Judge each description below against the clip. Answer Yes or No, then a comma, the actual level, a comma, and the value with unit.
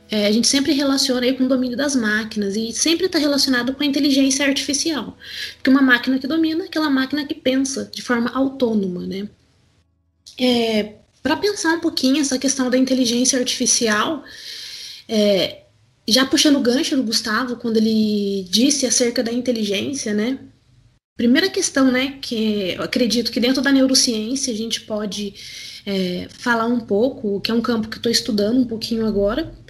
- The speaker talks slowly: No, average, 170 wpm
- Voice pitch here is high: Yes, high, 245 Hz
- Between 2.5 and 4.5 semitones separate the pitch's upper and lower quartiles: Yes, average, 4.0 semitones